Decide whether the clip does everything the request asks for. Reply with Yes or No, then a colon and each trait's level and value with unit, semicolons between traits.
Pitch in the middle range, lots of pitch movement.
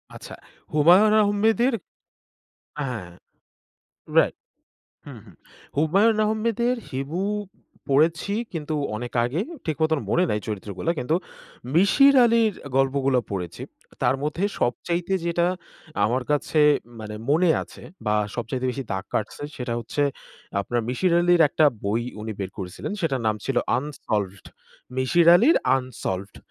Yes: medium, 145 Hz; wide, 6.8 semitones